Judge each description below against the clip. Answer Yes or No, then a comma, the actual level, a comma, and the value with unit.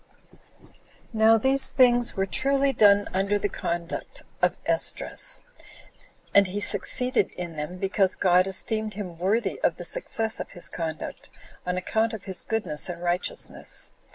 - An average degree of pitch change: Yes, average, 3.8 semitones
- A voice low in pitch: No, high, 200 Hz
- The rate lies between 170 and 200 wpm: No, average, 150 wpm